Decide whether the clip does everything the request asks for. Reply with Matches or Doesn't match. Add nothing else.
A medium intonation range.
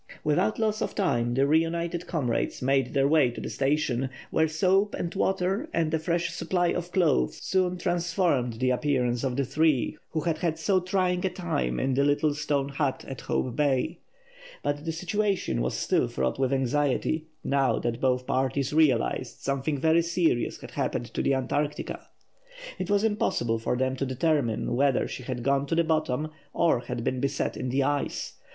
Matches